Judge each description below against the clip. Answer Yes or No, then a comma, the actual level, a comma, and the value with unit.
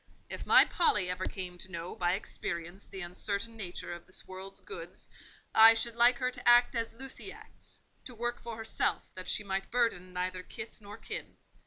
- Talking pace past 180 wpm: Yes, average, 190 wpm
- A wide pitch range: No, average, 4.2 semitones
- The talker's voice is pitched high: Yes, high, 200 Hz